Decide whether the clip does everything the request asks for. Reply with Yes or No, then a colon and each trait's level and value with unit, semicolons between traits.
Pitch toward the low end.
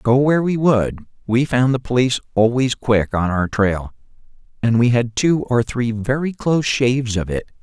Yes: low, 120 Hz